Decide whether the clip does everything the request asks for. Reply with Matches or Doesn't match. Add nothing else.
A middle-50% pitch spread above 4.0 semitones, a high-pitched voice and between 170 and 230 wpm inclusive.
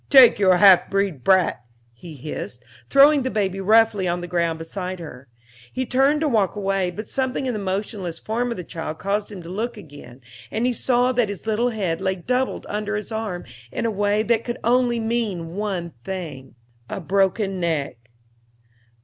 Matches